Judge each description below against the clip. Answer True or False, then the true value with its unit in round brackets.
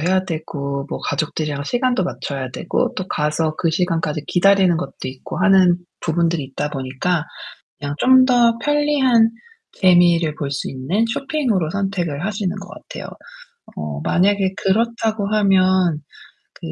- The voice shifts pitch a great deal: False (4.9 semitones)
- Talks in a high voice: False (180 Hz)